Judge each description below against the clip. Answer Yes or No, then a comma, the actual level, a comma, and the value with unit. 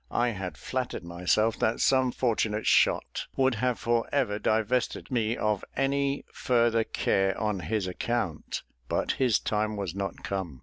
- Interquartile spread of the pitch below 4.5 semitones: Yes, average, 4.0 semitones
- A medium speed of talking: Yes, average, 150 wpm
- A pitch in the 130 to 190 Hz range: No, low, 110 Hz